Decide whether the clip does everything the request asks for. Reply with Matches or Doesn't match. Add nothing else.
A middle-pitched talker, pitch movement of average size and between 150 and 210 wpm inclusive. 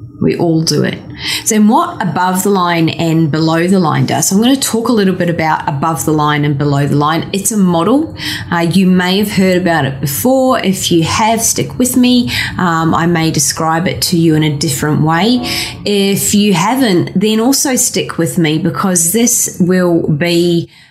Matches